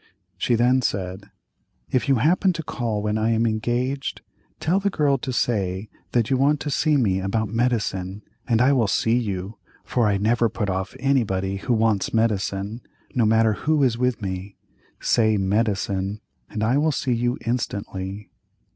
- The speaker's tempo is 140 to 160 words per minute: No, average, 170 wpm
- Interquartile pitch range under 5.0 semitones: Yes, average, 4.0 semitones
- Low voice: Yes, low, 115 Hz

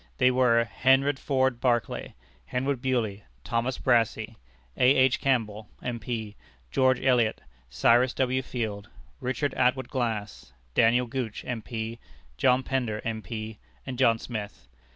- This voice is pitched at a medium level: No, low, 120 Hz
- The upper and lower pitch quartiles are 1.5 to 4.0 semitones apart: Yes, average, 2.7 semitones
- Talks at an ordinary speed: No, slow, 120 wpm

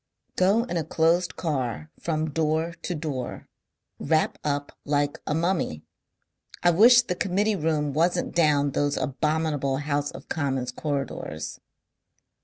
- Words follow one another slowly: Yes, slow, 130 wpm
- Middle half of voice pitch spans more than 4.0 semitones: No, average, 3.1 semitones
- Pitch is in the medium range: Yes, medium, 155 Hz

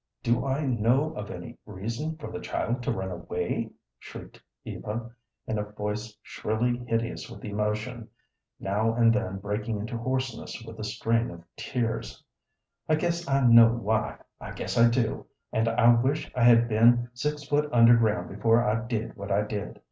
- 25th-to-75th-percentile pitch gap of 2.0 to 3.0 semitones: Yes, narrow, 2.5 semitones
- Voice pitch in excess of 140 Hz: No, low, 115 Hz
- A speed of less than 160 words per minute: No, average, 170 wpm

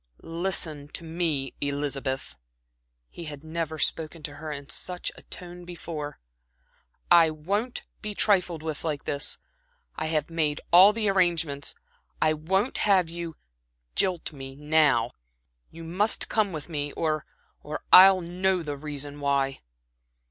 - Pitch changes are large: No, average, 3.3 semitones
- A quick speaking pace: No, average, 140 wpm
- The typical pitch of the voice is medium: Yes, medium, 160 Hz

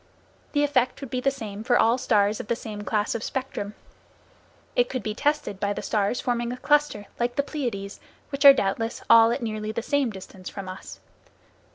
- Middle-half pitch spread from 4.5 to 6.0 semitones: No, average, 4.1 semitones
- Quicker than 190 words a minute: Yes, average, 200 wpm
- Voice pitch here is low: No, high, 230 Hz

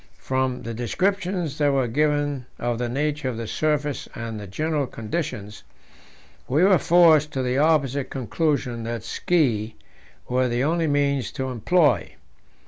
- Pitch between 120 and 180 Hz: Yes, medium, 140 Hz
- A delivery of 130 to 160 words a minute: Yes, average, 145 wpm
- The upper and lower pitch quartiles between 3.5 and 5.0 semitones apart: Yes, average, 4.1 semitones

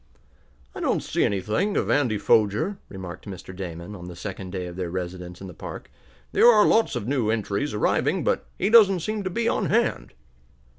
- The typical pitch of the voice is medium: No, low, 100 Hz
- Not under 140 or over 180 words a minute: No, average, 195 wpm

